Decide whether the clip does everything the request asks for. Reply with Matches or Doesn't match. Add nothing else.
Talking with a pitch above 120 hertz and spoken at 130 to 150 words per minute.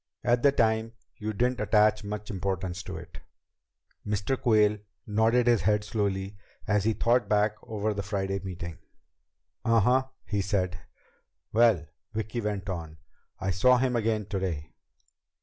Doesn't match